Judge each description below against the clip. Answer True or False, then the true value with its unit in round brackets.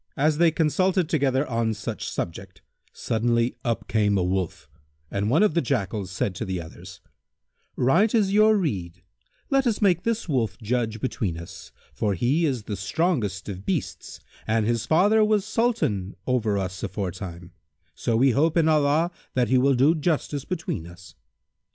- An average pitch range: False (8.6 semitones)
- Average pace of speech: True (165 wpm)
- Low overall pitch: True (120 Hz)